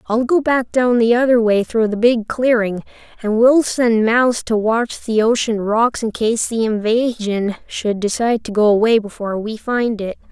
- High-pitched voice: Yes, high, 225 Hz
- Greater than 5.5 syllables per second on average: No, 4.6 syllables/s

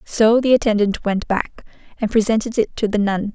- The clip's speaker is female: Yes, female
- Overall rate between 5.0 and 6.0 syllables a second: Yes, 5.1 syllables/s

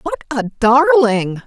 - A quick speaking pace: No, slow, 125 wpm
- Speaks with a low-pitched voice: No, very high, 255 Hz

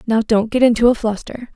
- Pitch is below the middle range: No, high, 230 Hz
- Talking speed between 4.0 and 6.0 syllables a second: Yes, 5.7 syllables/s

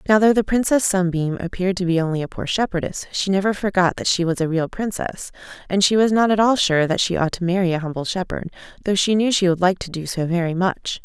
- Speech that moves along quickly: Yes, fast, 255 wpm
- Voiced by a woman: Yes, female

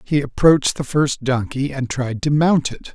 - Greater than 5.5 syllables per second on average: No, 4.6 syllables/s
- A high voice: No, medium, 140 Hz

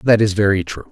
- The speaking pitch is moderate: No, low, 100 Hz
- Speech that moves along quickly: Yes, fast, 260 wpm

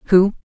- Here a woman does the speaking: Yes, female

